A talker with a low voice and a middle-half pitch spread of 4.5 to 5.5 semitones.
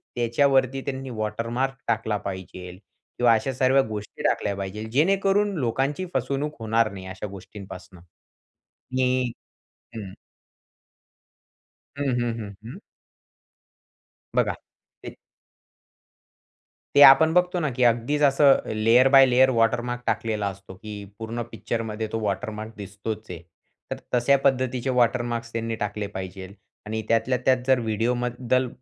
No: low, 115 Hz; average, 3.6 semitones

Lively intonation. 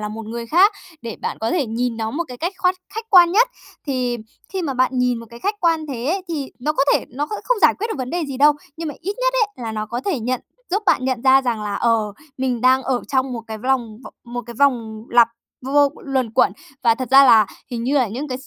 No: average, 4.5 semitones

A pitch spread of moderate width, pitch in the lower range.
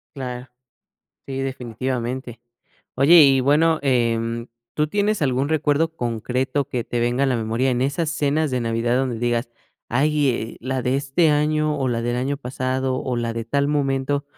Yes: average, 3.1 semitones; low, 130 Hz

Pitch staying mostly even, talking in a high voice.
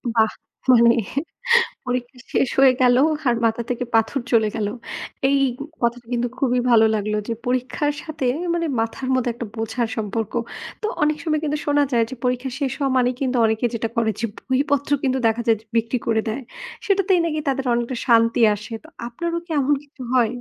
No: average, 3.2 semitones; high, 245 Hz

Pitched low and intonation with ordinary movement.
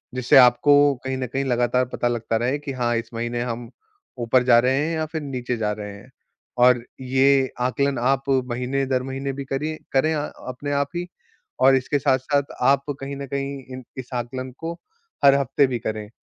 No: low, 130 Hz; narrow, 2.2 semitones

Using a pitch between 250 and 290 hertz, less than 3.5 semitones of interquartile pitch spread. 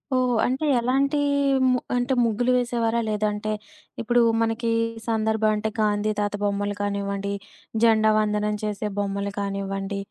No: high, 215 Hz; narrow, 2.5 semitones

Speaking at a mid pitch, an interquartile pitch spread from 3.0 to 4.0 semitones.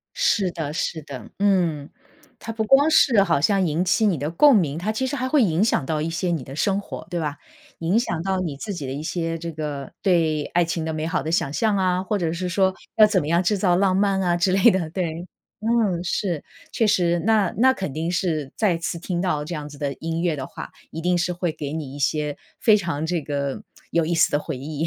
Yes: medium, 170 Hz; average, 3.7 semitones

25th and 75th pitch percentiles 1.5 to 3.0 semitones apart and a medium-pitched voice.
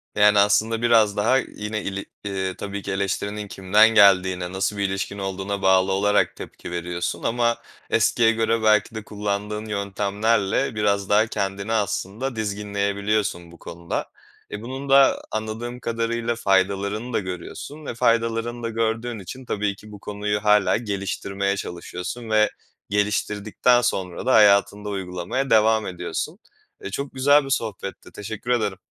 No: narrow, 2.5 semitones; low, 105 Hz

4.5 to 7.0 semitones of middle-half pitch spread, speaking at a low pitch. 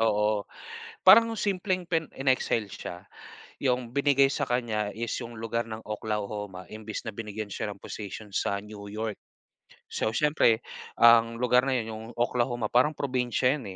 No: average, 3.1 semitones; low, 115 Hz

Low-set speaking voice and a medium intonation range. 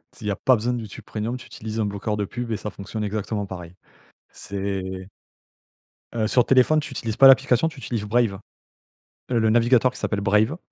Yes: low, 110 Hz; average, 3.2 semitones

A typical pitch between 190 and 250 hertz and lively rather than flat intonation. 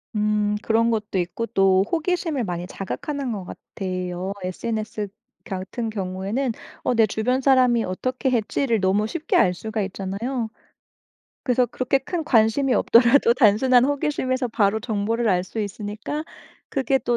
No: high, 225 Hz; average, 4.3 semitones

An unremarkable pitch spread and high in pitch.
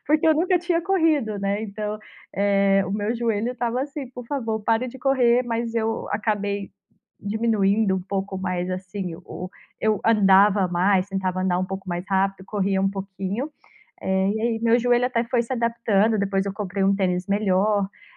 Yes: average, 3.4 semitones; high, 205 Hz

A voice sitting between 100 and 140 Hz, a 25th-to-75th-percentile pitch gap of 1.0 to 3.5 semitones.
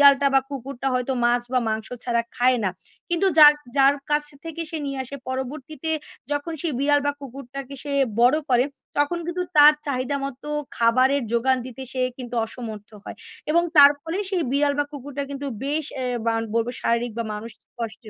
No: very high, 275 Hz; average, 3.0 semitones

